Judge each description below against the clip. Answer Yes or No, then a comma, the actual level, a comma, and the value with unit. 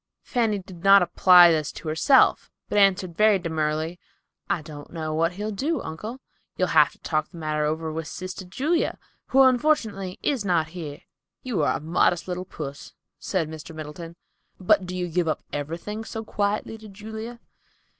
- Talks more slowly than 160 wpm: No, average, 175 wpm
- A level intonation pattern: No, average, 4.8 semitones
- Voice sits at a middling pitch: Yes, medium, 180 Hz